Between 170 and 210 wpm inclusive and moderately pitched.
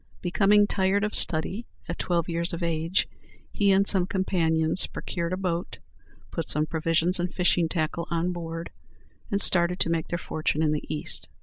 Yes: average, 175 wpm; medium, 170 Hz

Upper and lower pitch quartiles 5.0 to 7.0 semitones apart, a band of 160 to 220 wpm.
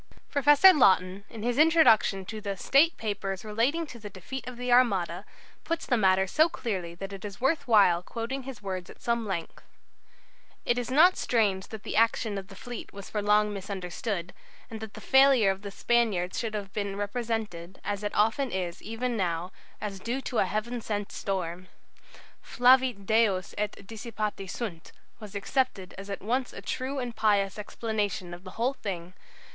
No: average, 4.0 semitones; average, 180 wpm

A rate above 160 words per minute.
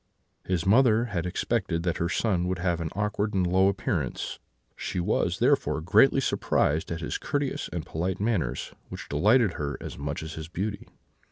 Yes: average, 180 wpm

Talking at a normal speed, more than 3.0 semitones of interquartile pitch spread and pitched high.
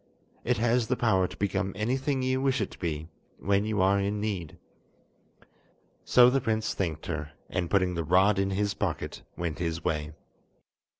No: average, 175 wpm; average, 4.5 semitones; low, 100 Hz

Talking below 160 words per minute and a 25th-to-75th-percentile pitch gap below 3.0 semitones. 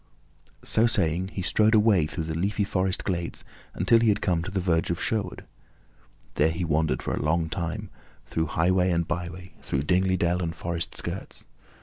No: average, 185 wpm; narrow, 2.6 semitones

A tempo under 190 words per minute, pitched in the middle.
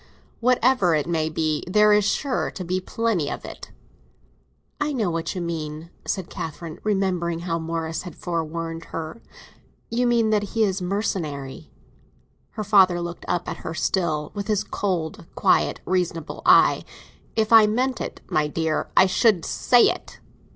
Yes: average, 160 wpm; medium, 180 Hz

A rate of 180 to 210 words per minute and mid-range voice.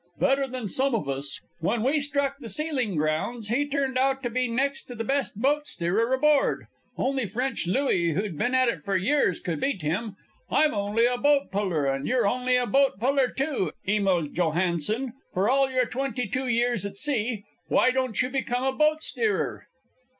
No: average, 190 wpm; high, 245 Hz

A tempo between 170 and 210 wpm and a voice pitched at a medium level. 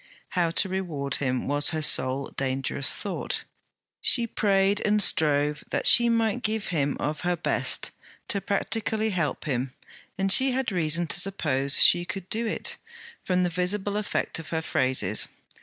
No: average, 160 wpm; medium, 175 Hz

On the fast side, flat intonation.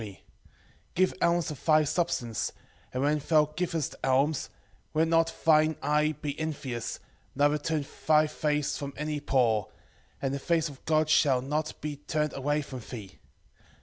No: average, 155 wpm; narrow, 2.2 semitones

